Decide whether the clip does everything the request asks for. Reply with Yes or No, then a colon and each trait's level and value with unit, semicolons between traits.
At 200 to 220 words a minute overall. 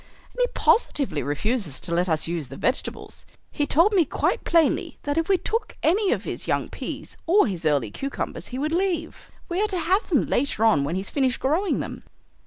Yes: fast, 205 wpm